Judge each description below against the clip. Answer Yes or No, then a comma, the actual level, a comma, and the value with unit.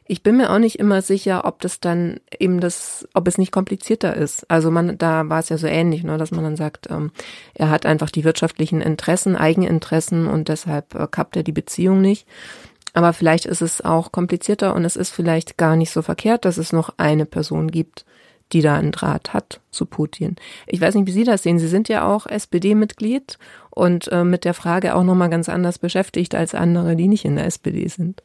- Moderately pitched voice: Yes, medium, 175 Hz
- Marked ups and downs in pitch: No, average, 2.7 semitones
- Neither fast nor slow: No, fast, 210 wpm